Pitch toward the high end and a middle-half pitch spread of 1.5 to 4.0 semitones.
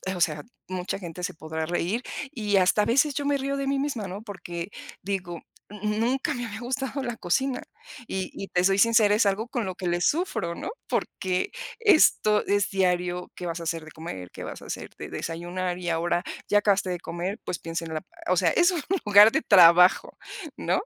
No: high, 195 Hz; average, 4.8 semitones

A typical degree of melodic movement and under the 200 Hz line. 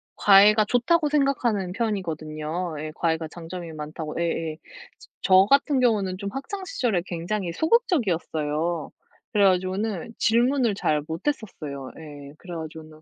No: wide, 6.1 semitones; medium, 185 Hz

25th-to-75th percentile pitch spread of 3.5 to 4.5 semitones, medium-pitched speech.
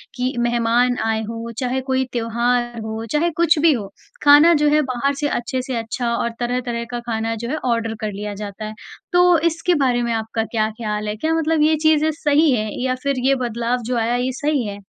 No: average, 4.0 semitones; high, 245 Hz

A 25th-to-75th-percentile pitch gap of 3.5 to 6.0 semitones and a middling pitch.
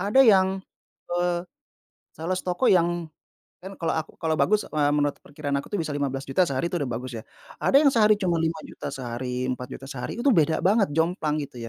Yes: average, 4.9 semitones; medium, 160 Hz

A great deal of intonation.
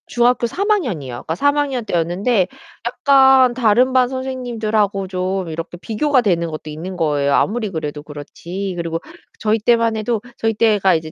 Yes: wide, 6.4 semitones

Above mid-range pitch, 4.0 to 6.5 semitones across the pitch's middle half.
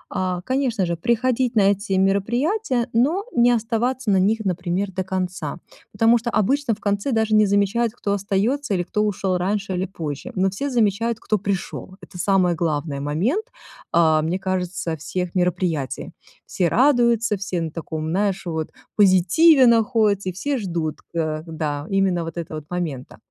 Yes: high, 195 Hz; average, 4.6 semitones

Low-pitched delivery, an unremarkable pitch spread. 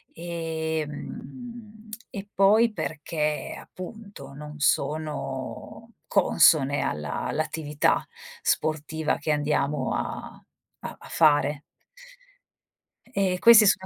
No: medium, 160 Hz; average, 5.0 semitones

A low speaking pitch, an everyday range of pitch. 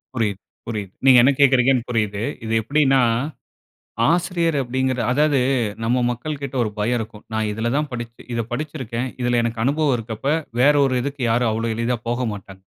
Yes: low, 120 Hz; average, 3.3 semitones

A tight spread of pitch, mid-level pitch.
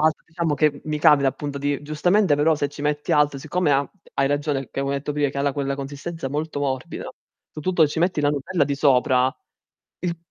Yes: narrow, 1.8 semitones; medium, 145 Hz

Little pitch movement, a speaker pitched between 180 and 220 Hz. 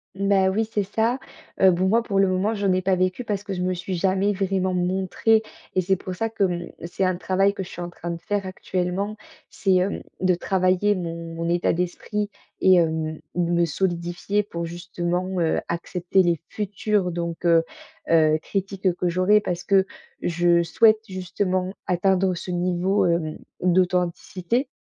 Yes: narrow, 2.1 semitones; medium, 185 Hz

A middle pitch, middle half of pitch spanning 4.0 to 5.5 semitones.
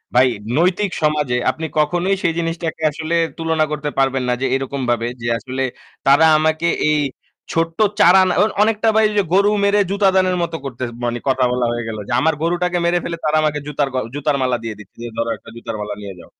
Yes: medium, 155 Hz; average, 5.1 semitones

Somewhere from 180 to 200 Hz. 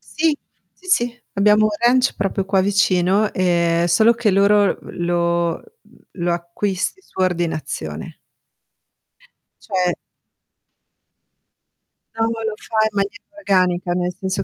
Yes: high, 190 Hz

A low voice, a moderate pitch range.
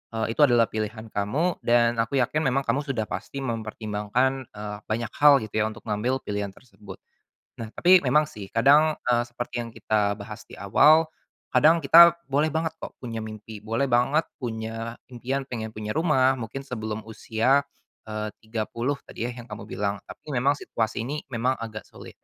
Yes: low, 120 Hz; average, 3.9 semitones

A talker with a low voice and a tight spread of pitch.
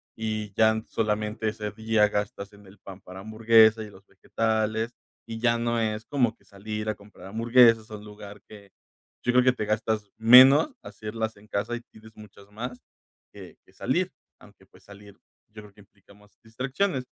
Yes: low, 110 Hz; narrow, 1.7 semitones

